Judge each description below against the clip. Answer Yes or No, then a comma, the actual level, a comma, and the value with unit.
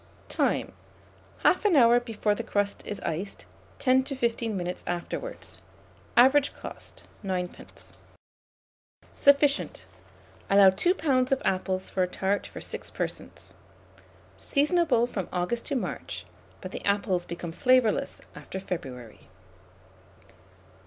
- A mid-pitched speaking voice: No, high, 210 Hz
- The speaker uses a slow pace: Yes, slow, 115 wpm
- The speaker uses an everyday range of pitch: No, wide, 5.9 semitones